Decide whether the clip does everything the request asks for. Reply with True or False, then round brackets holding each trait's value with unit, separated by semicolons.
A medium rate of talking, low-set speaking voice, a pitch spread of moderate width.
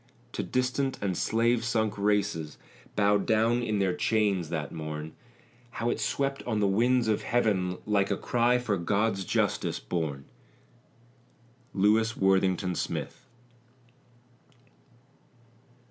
False (115 wpm; 105 Hz; 3.8 semitones)